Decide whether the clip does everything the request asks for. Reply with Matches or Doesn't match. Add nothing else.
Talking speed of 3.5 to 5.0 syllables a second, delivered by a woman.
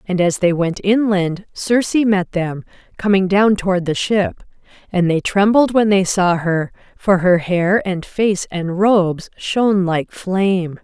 Matches